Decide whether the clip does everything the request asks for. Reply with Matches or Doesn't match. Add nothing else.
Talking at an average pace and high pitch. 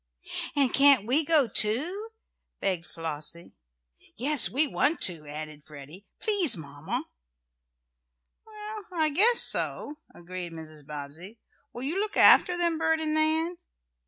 Doesn't match